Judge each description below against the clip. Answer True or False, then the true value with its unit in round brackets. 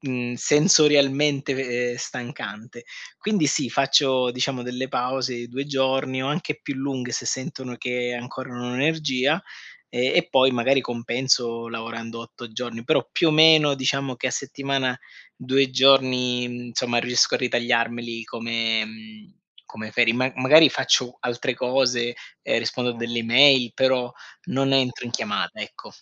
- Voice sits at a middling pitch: False (125 Hz)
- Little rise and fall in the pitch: True (2.1 semitones)